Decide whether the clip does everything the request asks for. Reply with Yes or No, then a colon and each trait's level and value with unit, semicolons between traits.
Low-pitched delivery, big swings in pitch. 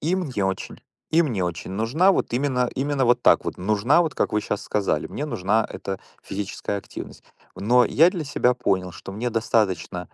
Yes: low, 115 Hz; wide, 6.3 semitones